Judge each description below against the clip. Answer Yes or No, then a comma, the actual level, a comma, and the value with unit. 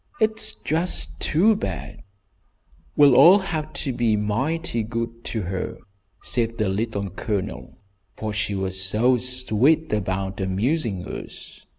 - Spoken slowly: Yes, slow, 125 wpm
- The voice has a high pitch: No, low, 115 Hz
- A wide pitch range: Yes, wide, 7.0 semitones